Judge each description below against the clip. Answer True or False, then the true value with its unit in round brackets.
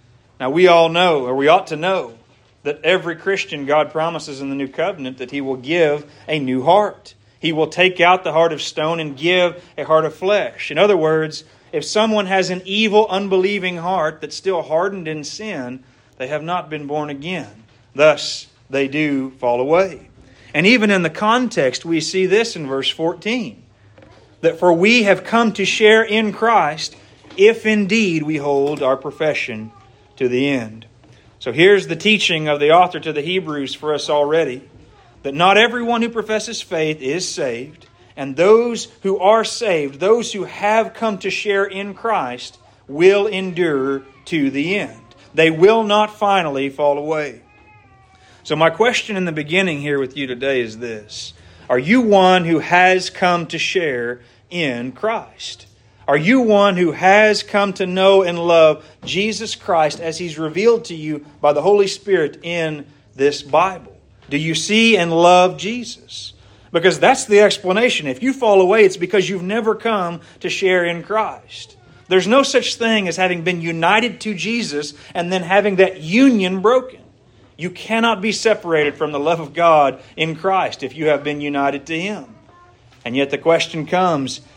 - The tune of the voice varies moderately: False (6.1 semitones)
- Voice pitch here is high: False (165 Hz)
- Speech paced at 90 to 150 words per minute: False (175 wpm)